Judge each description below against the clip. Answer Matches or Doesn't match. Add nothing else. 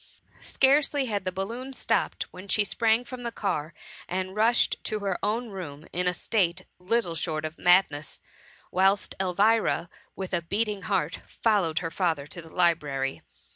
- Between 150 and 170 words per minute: Matches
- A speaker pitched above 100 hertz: Matches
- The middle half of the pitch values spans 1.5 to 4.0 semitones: Doesn't match